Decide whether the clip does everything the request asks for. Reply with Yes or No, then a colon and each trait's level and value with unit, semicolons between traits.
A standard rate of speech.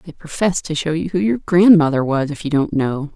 No: fast, 245 wpm